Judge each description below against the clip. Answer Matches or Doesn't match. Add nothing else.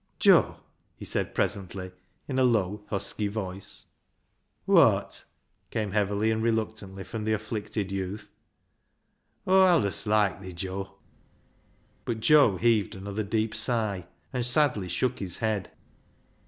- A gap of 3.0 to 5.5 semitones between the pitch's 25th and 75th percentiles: Doesn't match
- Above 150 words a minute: Doesn't match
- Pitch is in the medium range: Doesn't match